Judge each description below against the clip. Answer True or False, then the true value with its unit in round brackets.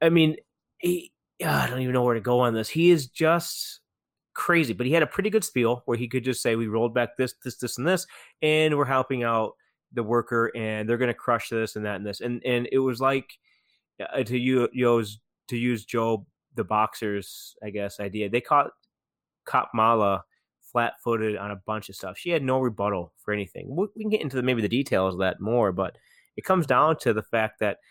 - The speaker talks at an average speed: False (230 wpm)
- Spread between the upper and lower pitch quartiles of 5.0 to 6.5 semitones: False (3.7 semitones)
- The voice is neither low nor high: False (120 Hz)